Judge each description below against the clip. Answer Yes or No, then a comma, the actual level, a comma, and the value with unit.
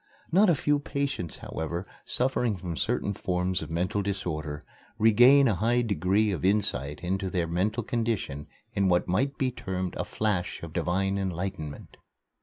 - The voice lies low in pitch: Yes, very low, 95 Hz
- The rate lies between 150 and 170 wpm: Yes, average, 155 wpm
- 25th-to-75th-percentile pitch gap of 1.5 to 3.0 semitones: No, average, 4.4 semitones